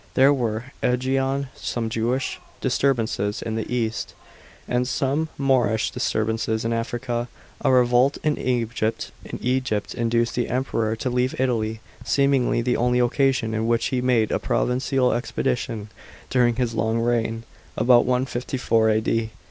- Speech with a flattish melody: Yes, narrow, 2.3 semitones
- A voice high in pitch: No, low, 120 Hz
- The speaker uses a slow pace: Yes, slow, 130 wpm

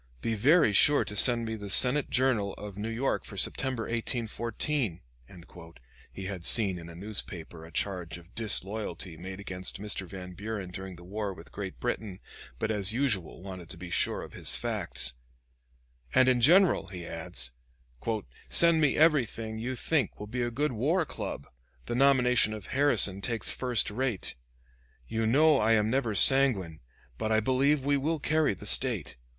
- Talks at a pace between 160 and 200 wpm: Yes, average, 170 wpm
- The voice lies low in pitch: Yes, low, 110 Hz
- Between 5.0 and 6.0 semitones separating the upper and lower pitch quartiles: Yes, average, 5.3 semitones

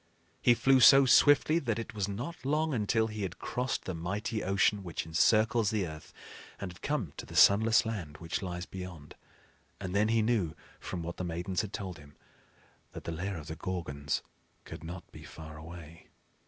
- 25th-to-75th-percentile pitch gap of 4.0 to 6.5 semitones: Yes, average, 5.1 semitones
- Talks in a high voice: No, very low, 95 Hz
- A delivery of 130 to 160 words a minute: No, average, 190 wpm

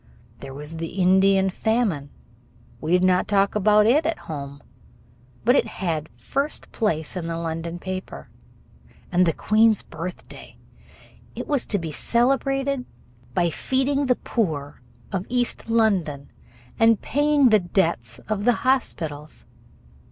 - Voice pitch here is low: No, high, 195 Hz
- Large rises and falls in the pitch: Yes, wide, 6.4 semitones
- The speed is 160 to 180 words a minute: No, slow, 135 wpm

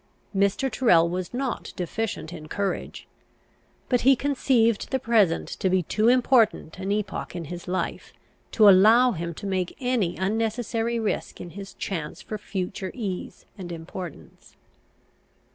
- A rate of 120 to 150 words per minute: Yes, average, 145 wpm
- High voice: Yes, high, 200 Hz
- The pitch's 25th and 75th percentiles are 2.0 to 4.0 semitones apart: No, average, 4.4 semitones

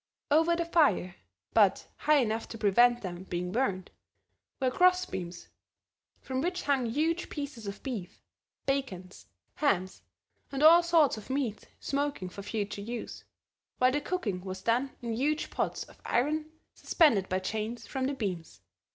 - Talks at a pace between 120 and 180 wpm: Yes, average, 150 wpm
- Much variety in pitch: Yes, wide, 6.7 semitones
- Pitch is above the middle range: Yes, high, 245 Hz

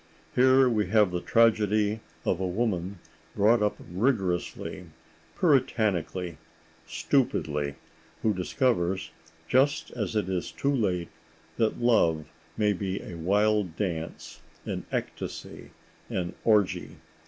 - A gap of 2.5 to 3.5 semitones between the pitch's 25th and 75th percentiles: No, average, 4.1 semitones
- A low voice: Yes, low, 105 Hz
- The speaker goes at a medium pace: No, slow, 110 wpm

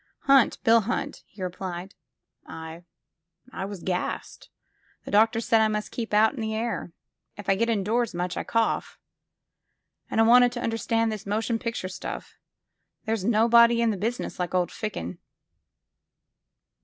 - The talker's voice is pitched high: Yes, high, 220 Hz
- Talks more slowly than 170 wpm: Yes, average, 160 wpm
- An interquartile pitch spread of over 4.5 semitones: No, average, 3.2 semitones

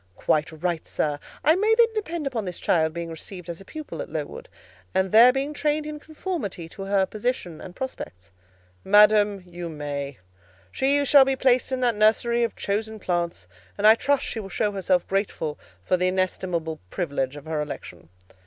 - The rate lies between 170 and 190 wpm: Yes, average, 180 wpm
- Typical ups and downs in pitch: No, wide, 7.4 semitones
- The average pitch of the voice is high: Yes, high, 200 Hz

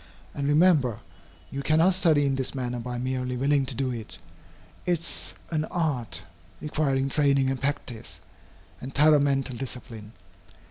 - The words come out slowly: No, average, 145 wpm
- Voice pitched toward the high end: No, low, 135 Hz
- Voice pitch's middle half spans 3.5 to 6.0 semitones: No, average, 3.0 semitones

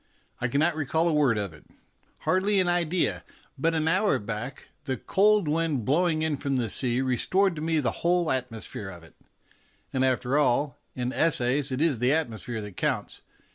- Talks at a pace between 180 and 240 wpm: Yes, average, 190 wpm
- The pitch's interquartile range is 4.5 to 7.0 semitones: Yes, average, 5.0 semitones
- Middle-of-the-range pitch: Yes, medium, 145 Hz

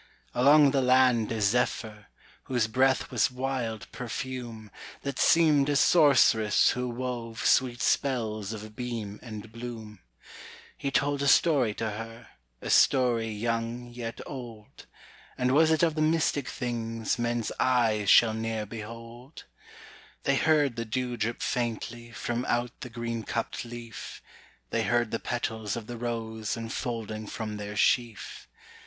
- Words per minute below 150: Yes, average, 140 wpm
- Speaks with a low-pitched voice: Yes, low, 120 Hz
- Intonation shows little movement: Yes, narrow, 2.3 semitones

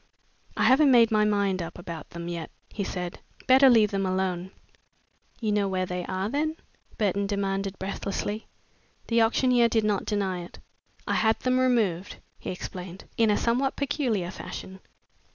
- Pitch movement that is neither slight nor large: Yes, average, 3.8 semitones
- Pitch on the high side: Yes, high, 200 Hz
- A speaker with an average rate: Yes, average, 165 wpm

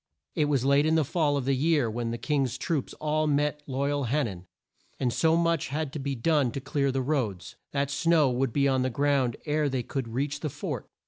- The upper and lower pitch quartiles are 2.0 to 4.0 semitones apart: Yes, narrow, 2.6 semitones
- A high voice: No, medium, 140 Hz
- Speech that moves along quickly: Yes, fast, 240 wpm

